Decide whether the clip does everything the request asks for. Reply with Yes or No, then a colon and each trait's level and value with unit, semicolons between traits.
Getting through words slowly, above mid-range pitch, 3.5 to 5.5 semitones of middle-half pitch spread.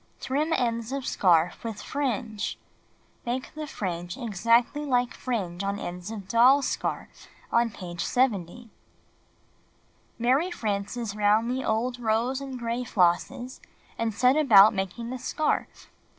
Yes: slow, 125 wpm; high, 230 Hz; average, 4.1 semitones